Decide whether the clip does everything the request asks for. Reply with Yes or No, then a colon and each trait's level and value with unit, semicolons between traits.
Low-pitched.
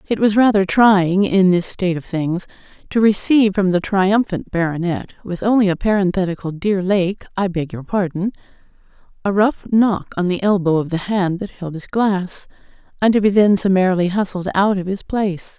No: high, 190 Hz